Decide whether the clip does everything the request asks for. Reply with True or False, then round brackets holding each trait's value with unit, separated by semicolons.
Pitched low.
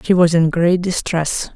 False (170 Hz)